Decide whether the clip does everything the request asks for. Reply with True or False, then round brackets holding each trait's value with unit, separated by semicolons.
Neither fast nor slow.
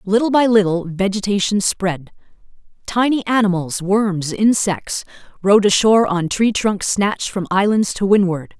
False (120 wpm)